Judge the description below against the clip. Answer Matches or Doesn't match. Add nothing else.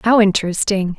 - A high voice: Matches